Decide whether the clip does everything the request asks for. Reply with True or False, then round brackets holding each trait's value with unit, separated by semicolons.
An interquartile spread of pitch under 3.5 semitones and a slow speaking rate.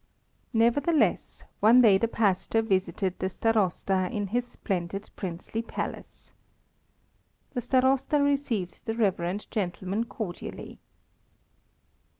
False (4.0 semitones; 100 wpm)